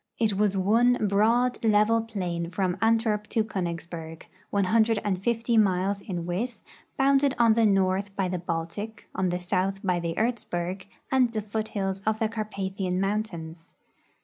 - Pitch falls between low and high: No, high, 200 Hz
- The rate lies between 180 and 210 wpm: No, average, 150 wpm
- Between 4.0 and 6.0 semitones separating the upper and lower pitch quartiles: No, average, 3.4 semitones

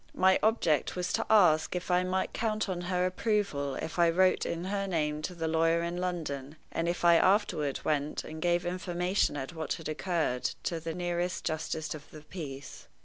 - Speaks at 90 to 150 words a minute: No, average, 195 wpm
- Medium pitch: Yes, medium, 170 Hz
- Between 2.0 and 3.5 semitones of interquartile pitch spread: Yes, average, 2.8 semitones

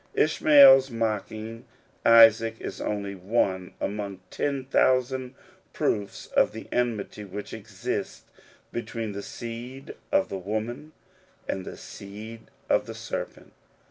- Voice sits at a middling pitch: No, low, 115 Hz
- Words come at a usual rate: No, slow, 120 wpm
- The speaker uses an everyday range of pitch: Yes, average, 3.7 semitones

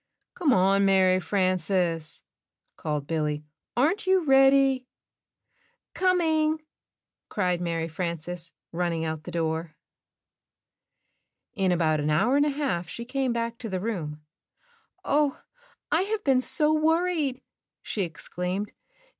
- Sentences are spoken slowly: Yes, slow, 120 wpm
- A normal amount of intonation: No, wide, 8.7 semitones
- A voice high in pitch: Yes, high, 195 Hz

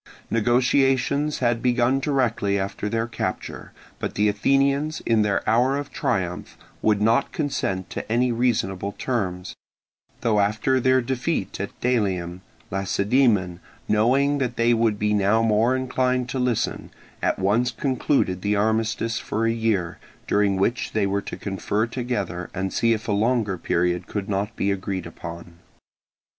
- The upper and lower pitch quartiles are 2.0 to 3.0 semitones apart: No, average, 4.1 semitones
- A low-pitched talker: Yes, low, 110 Hz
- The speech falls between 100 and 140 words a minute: No, average, 150 wpm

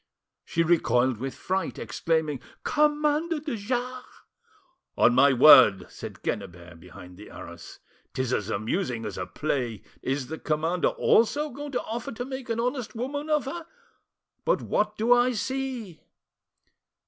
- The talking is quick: No, average, 145 wpm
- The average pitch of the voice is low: No, high, 190 Hz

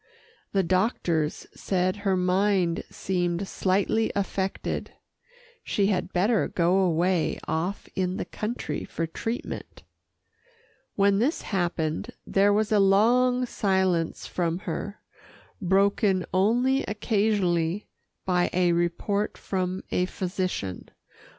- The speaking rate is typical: No, slow, 105 wpm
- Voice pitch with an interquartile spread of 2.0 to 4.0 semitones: Yes, narrow, 2.6 semitones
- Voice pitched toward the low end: No, high, 190 Hz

